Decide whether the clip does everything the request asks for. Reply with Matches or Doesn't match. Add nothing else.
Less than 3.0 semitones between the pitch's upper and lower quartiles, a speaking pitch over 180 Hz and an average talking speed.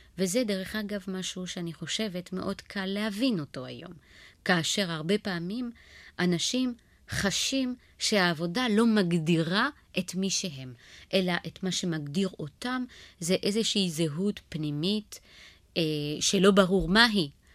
Doesn't match